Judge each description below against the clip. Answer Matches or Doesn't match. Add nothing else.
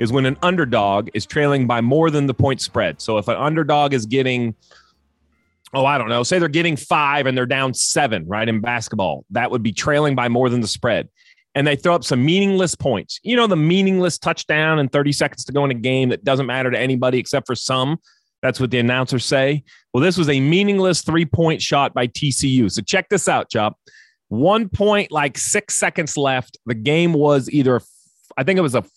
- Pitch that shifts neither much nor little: Matches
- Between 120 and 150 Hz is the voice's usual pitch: Matches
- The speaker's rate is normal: Doesn't match